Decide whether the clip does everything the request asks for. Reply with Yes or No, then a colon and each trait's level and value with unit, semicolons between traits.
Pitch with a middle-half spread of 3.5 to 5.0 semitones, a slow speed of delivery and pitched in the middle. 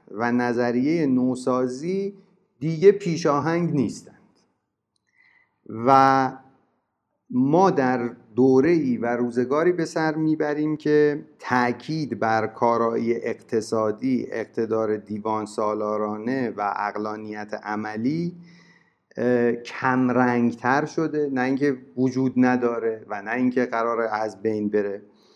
No: average, 4.7 semitones; slow, 95 wpm; low, 125 Hz